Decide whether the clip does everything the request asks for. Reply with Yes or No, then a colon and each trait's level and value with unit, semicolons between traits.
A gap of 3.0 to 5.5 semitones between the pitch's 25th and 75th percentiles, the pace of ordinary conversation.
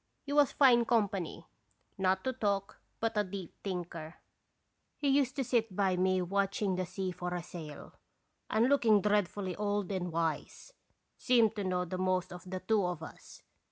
Yes: average, 3.5 semitones; average, 170 wpm